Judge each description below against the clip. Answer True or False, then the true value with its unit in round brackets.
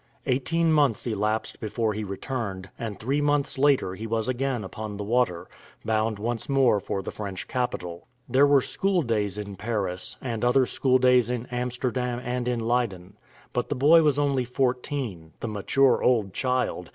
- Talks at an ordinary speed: True (170 wpm)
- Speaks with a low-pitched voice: True (120 Hz)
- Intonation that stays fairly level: False (3.8 semitones)